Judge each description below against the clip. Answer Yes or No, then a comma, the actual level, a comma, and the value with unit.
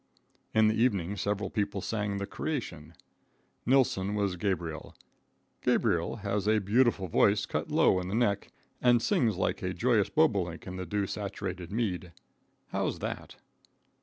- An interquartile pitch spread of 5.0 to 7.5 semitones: No, average, 3.0 semitones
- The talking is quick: No, average, 145 wpm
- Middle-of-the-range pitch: No, low, 100 Hz